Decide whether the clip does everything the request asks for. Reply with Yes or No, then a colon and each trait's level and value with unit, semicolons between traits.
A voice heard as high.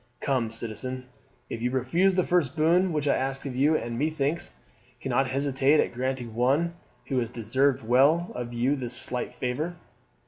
No: low, 135 Hz